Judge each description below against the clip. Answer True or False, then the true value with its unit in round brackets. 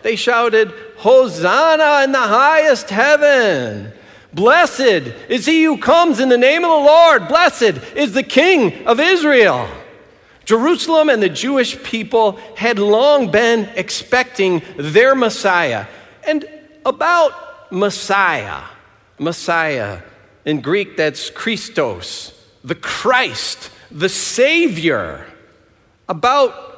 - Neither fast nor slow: False (110 wpm)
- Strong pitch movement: True (7.1 semitones)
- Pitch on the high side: True (245 Hz)